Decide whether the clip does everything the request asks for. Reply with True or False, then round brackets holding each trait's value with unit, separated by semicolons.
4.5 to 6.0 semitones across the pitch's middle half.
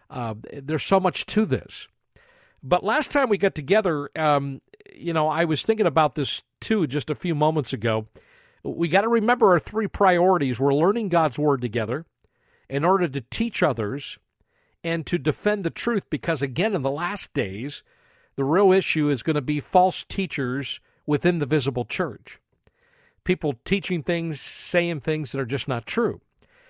True (5.0 semitones)